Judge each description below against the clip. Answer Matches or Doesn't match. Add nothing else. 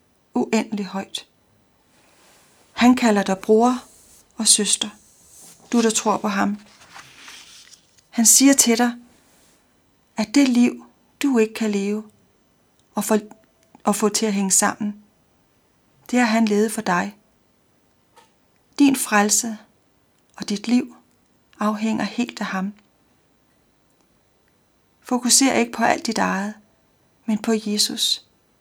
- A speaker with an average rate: Doesn't match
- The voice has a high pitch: Matches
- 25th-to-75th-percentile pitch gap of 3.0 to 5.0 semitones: Doesn't match